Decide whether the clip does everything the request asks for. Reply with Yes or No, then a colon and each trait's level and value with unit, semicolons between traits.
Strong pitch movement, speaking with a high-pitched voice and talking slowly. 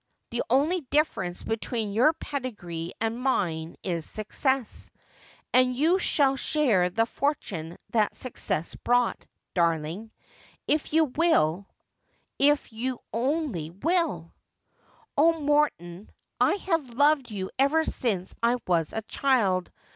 Yes: wide, 7.9 semitones; high, 240 Hz; slow, 125 wpm